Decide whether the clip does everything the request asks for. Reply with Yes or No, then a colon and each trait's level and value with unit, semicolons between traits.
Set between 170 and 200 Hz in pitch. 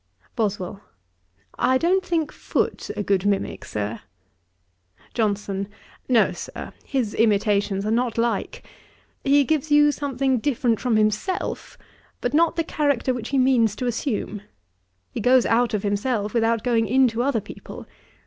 No: high, 235 Hz